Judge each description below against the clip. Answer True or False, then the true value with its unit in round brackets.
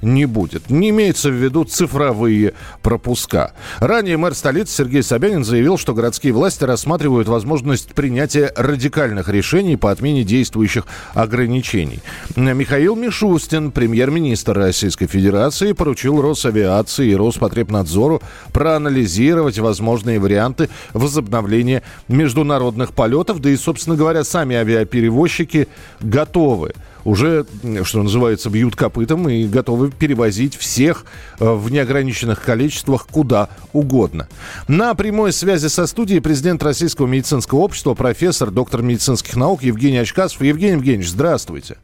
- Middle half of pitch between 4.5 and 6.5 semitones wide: True (5.2 semitones)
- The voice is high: False (130 Hz)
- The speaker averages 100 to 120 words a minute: True (115 wpm)